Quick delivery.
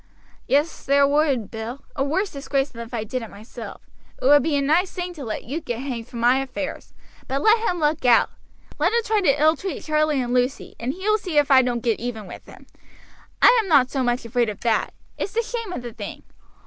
Yes: fast, 240 wpm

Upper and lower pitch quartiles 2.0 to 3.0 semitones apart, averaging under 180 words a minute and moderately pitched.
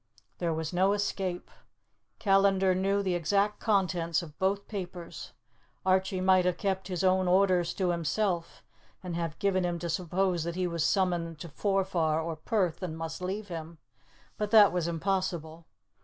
Yes: narrow, 2.4 semitones; average, 160 wpm; medium, 180 Hz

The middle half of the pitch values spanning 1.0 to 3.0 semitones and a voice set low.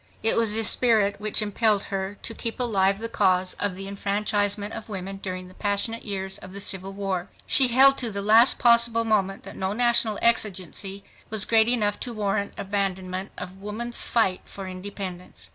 No: narrow, 2.6 semitones; high, 205 Hz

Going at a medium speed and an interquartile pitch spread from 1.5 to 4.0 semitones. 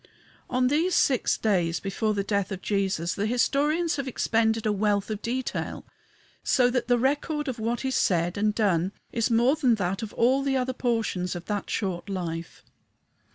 No: average, 180 wpm; average, 4.7 semitones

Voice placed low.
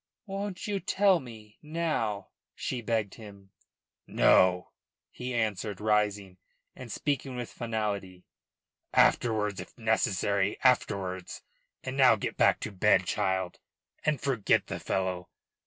Yes: low, 110 Hz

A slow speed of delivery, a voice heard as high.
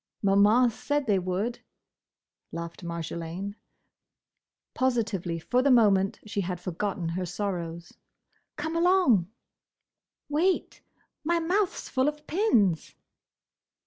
Yes: slow, 105 wpm; high, 205 Hz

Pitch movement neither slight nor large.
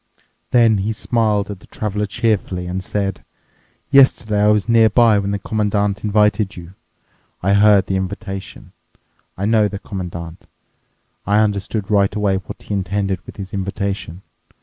No: narrow, 1.7 semitones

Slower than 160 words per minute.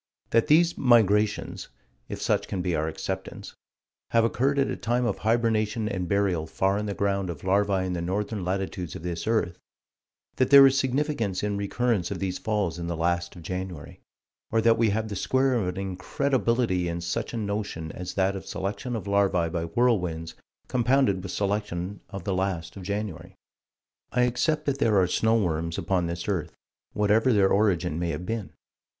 No: average, 185 wpm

